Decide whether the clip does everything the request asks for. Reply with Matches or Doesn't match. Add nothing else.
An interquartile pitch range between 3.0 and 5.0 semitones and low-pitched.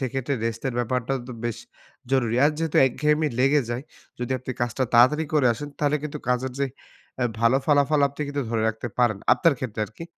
Matches